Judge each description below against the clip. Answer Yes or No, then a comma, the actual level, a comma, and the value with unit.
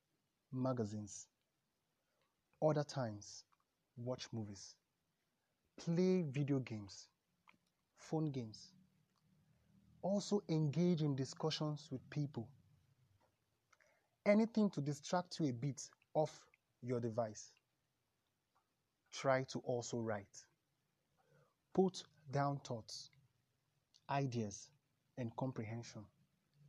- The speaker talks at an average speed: No, slow, 80 wpm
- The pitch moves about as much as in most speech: Yes, average, 4.5 semitones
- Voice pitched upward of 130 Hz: Yes, medium, 140 Hz